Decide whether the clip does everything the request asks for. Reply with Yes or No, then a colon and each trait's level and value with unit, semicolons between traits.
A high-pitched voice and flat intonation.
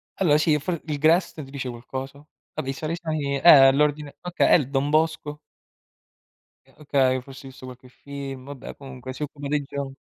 No: medium, 140 Hz; narrow, 2.1 semitones